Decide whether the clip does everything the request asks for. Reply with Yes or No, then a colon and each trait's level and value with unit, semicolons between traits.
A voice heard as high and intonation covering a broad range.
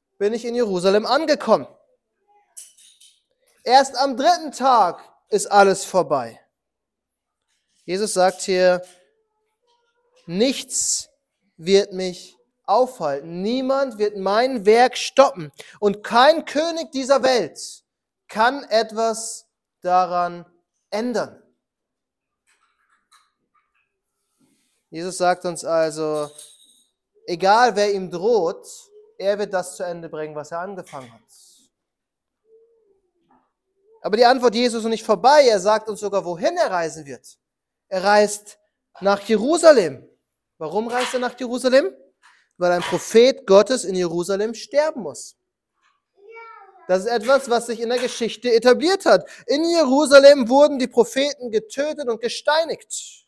Yes: high, 235 Hz; wide, 7.4 semitones